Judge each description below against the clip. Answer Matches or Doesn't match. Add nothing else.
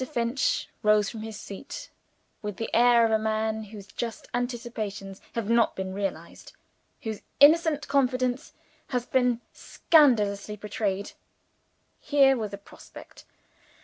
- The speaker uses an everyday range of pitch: Matches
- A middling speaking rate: Doesn't match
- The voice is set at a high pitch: Matches